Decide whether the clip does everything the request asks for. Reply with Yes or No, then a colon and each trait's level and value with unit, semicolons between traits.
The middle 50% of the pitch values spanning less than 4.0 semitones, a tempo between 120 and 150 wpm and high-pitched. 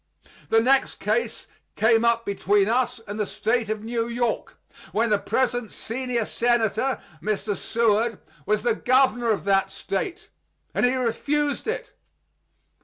Yes: average, 2.7 semitones; average, 140 wpm; high, 230 Hz